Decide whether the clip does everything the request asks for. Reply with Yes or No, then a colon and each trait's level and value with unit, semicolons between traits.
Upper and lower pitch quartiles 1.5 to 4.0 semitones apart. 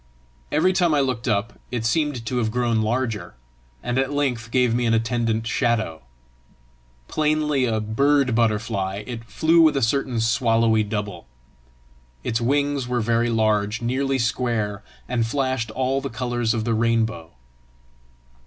Yes: average, 2.9 semitones